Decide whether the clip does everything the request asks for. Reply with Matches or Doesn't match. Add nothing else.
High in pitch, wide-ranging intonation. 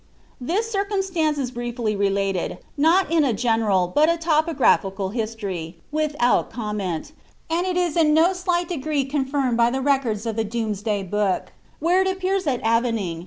Matches